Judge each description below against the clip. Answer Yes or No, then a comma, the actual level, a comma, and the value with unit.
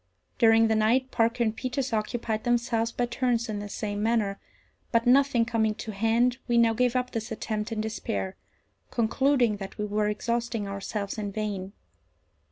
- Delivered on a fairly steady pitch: Yes, narrow, 2.1 semitones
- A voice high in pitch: Yes, high, 225 Hz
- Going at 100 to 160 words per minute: No, average, 170 wpm